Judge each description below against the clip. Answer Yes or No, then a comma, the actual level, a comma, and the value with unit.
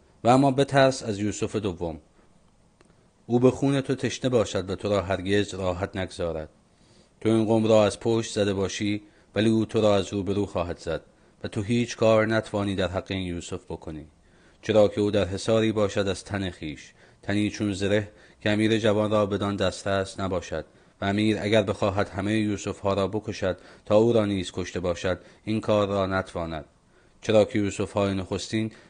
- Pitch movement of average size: No, narrow, 2.3 semitones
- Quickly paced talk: Yes, fast, 185 wpm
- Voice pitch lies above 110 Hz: No, low, 100 Hz